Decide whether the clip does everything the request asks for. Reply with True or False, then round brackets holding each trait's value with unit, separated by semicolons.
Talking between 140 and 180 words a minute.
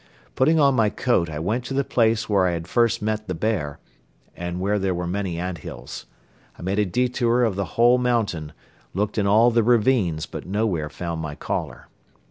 False (200 wpm)